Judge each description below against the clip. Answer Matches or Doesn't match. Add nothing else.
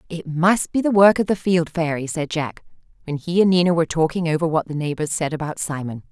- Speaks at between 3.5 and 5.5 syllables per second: Doesn't match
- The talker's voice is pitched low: Doesn't match